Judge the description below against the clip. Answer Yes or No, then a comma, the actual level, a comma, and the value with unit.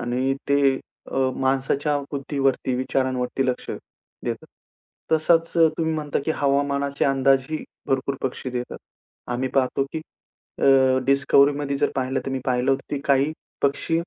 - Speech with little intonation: Yes, narrow, 1.4 semitones